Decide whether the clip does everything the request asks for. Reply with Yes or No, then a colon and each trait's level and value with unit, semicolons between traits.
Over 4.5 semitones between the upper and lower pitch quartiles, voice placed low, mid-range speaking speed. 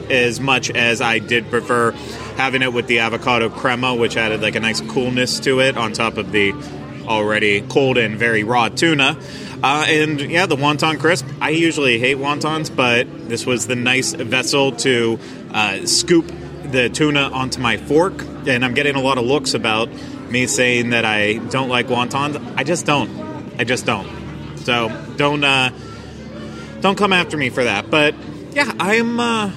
No: average, 3.9 semitones; low, 130 Hz; average, 180 wpm